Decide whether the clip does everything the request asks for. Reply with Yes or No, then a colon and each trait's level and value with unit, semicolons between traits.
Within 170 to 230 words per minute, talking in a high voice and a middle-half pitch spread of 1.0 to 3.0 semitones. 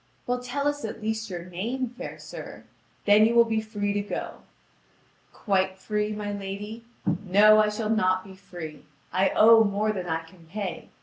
Yes: average, 180 wpm; high, 210 Hz; average, 2.7 semitones